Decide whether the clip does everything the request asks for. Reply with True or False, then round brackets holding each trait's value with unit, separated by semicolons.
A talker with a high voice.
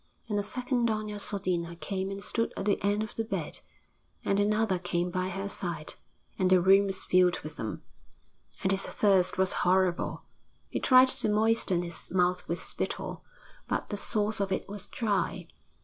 True (195 Hz)